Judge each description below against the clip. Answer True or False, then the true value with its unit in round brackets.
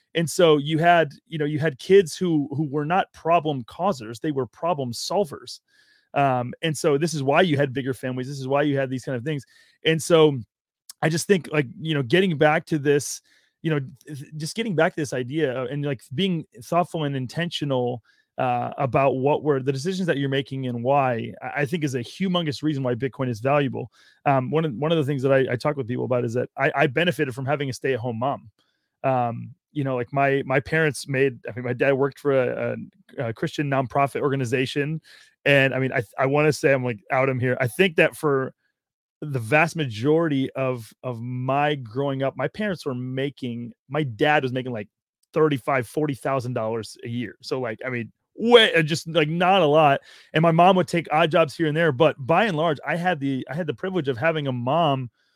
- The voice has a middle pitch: True (145 Hz)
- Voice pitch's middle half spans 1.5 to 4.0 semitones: True (3.6 semitones)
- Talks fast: True (225 wpm)